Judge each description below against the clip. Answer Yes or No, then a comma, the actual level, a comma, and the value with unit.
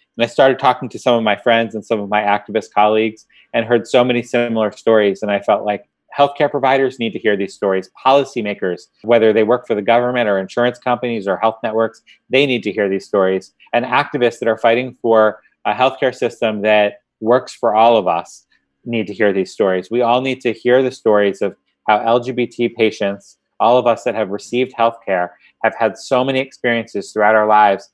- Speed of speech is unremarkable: No, fast, 210 wpm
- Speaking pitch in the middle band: No, low, 115 Hz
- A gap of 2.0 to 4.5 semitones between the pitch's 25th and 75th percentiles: Yes, average, 2.9 semitones